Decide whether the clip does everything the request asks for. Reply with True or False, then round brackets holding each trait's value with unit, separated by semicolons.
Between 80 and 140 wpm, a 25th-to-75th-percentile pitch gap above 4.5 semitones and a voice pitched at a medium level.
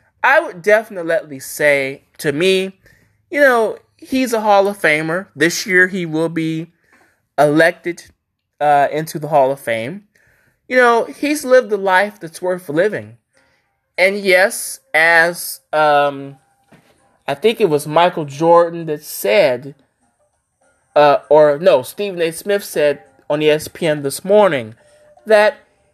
True (135 wpm; 5.4 semitones; 165 Hz)